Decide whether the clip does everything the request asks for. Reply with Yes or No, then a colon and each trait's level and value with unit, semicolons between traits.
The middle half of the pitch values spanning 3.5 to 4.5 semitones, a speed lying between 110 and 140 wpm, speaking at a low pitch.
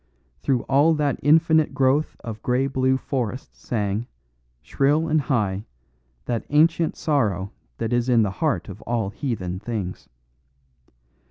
No: average, 5.3 semitones; slow, 135 wpm; low, 125 Hz